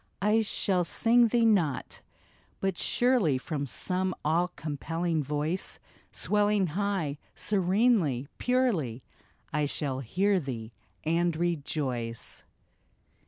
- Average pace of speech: No, slow, 100 wpm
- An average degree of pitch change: No, wide, 5.8 semitones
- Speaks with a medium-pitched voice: Yes, medium, 170 Hz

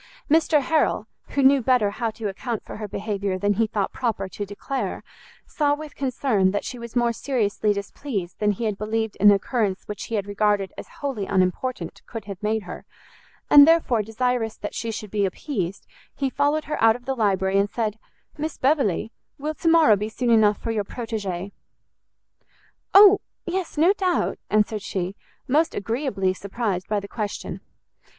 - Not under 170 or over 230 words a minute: Yes, average, 175 wpm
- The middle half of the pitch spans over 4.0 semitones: Yes, average, 4.7 semitones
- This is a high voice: Yes, high, 220 Hz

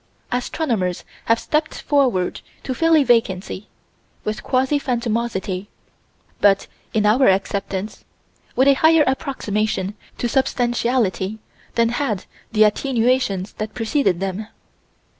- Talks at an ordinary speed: No, slow, 110 wpm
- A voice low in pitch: No, high, 230 Hz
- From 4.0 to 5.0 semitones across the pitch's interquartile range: Yes, average, 4.7 semitones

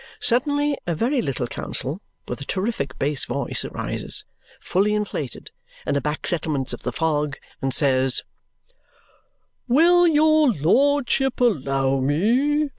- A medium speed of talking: No, slow, 125 wpm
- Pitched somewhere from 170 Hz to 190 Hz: Yes, medium, 185 Hz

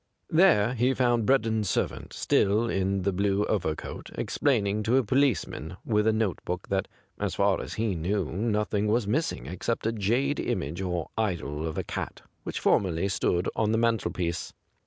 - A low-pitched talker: Yes, low, 105 Hz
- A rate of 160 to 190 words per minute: Yes, average, 170 wpm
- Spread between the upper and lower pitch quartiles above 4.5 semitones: No, average, 3.9 semitones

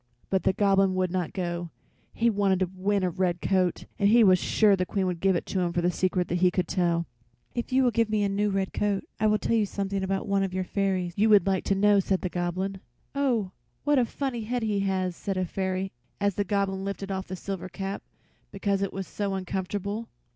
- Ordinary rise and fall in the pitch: No, narrow, 1.7 semitones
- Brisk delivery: Yes, fast, 235 wpm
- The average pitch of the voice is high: Yes, high, 195 Hz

